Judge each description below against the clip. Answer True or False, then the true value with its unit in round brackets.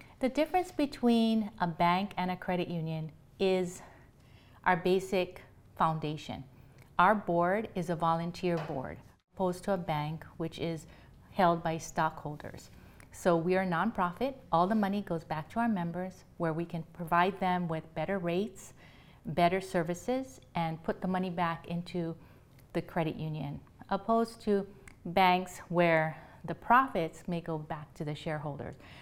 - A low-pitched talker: False (175 Hz)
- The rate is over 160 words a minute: False (150 wpm)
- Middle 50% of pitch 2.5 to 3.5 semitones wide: True (2.9 semitones)